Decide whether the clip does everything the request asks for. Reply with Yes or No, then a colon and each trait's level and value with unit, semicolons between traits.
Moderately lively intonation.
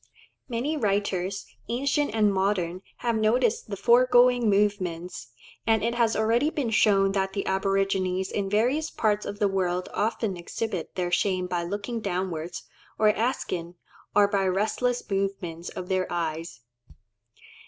Yes: average, 3.4 semitones